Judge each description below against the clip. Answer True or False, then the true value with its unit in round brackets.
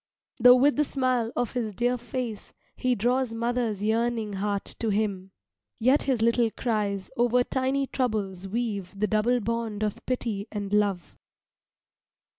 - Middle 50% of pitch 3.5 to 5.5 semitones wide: False (3.0 semitones)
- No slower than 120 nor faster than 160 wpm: True (145 wpm)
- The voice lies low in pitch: False (230 Hz)